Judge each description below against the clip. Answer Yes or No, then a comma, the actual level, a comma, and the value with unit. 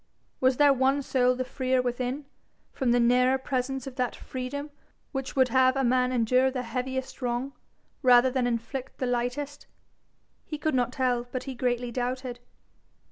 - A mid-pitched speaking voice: No, very high, 255 Hz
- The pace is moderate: Yes, average, 165 wpm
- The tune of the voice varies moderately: No, narrow, 1.2 semitones